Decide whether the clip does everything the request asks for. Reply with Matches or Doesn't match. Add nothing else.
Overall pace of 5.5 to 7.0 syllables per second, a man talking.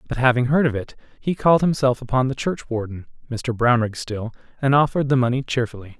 Matches